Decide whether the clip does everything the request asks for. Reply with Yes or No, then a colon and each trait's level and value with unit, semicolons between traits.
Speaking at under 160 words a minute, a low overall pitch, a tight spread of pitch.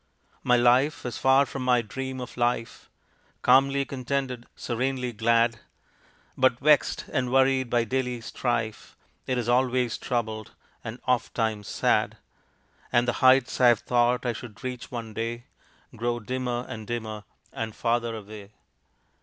Yes: average, 140 wpm; low, 120 Hz; narrow, 1.9 semitones